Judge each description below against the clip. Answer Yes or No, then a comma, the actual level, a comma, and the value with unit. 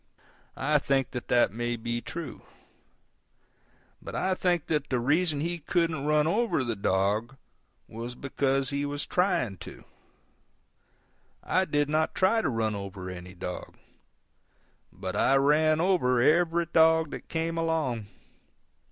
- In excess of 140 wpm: No, slow, 135 wpm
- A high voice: No, medium, 145 Hz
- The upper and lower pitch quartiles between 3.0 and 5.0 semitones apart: No, wide, 5.5 semitones